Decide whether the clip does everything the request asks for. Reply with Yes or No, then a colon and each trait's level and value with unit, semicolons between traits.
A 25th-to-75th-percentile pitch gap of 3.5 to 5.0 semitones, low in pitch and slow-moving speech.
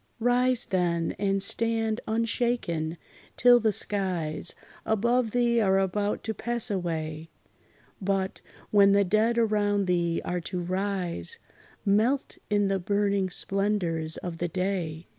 No: average, 3.8 semitones; high, 200 Hz; slow, 125 wpm